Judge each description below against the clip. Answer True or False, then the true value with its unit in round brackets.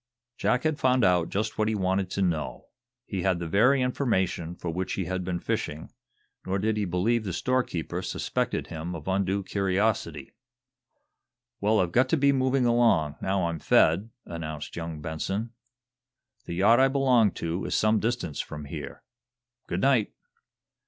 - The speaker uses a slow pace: False (165 wpm)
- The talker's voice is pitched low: True (95 Hz)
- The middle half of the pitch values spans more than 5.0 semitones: True (5.4 semitones)